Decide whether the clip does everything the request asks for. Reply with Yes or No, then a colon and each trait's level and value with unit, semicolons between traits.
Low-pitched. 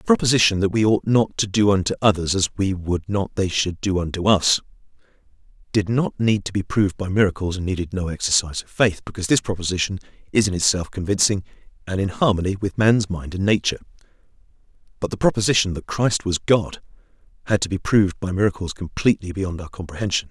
Yes: very low, 95 Hz